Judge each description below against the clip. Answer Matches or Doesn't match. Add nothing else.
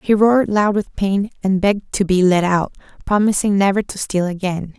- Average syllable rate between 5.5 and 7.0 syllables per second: Doesn't match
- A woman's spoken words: Matches